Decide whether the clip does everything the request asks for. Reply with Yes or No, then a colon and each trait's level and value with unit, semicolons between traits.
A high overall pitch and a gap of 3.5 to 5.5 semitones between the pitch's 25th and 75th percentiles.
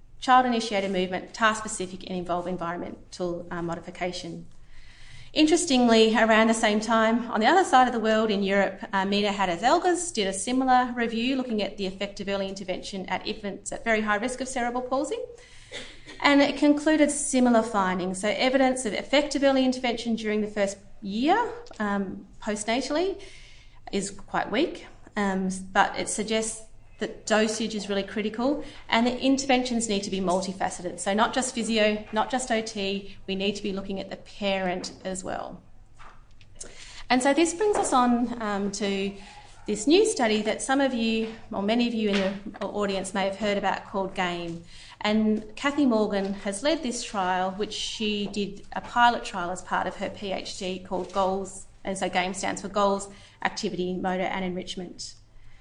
Yes: high, 210 Hz; average, 4.0 semitones